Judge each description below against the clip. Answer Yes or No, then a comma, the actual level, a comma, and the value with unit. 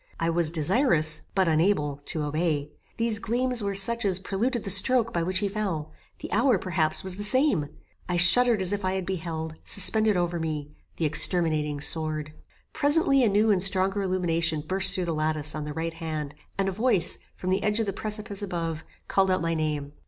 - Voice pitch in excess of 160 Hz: Yes, medium, 185 Hz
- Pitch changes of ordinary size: Yes, average, 4.5 semitones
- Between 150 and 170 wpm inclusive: No, average, 195 wpm